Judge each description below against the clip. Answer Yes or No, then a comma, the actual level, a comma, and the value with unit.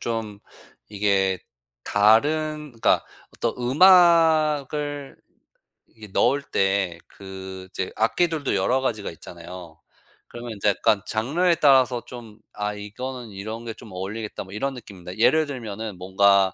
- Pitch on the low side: Yes, low, 110 Hz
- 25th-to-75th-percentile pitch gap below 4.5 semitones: No, wide, 5.6 semitones